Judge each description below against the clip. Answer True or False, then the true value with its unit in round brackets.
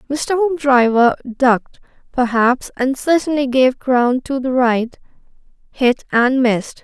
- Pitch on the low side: False (255 Hz)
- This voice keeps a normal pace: False (125 wpm)